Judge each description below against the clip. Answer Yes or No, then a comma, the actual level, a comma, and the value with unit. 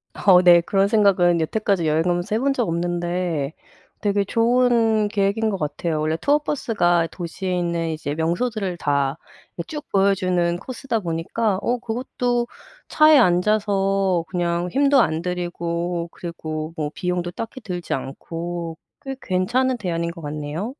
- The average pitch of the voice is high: No, medium, 180 Hz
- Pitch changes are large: No, average, 4.4 semitones